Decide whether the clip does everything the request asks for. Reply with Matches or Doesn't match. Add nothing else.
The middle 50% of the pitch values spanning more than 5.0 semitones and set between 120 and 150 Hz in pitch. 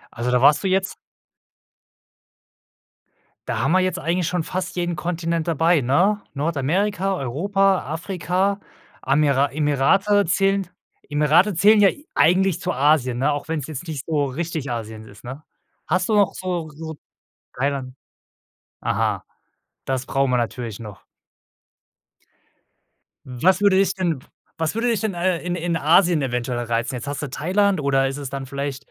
Doesn't match